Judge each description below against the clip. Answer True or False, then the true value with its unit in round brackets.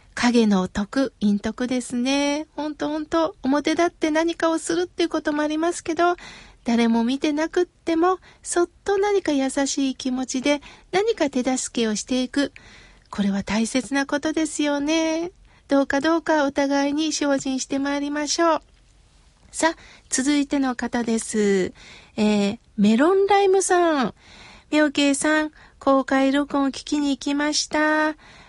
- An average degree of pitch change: True (3.6 semitones)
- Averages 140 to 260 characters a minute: False (280 characters per minute)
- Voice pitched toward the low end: False (290 Hz)